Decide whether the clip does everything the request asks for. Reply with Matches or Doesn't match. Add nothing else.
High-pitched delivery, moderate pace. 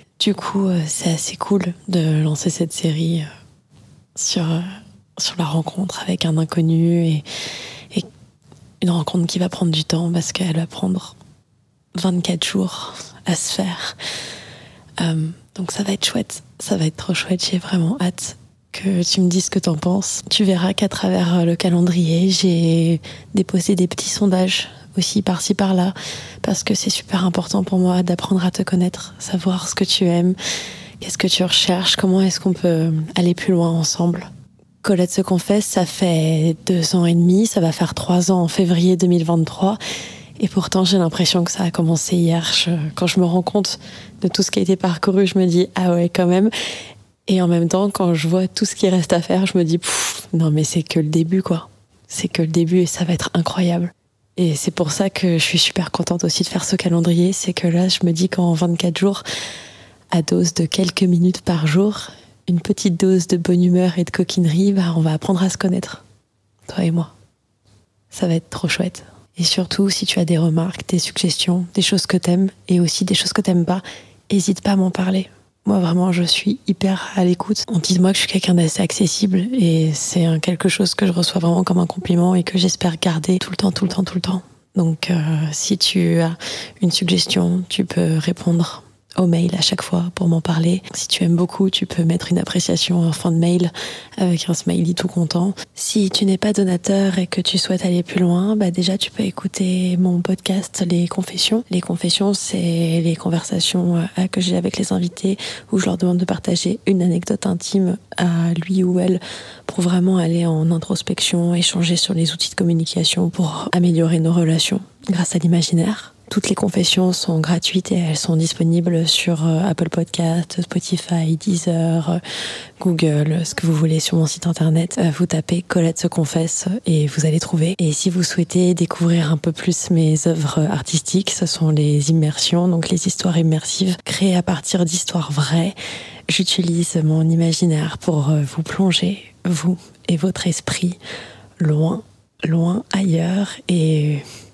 Doesn't match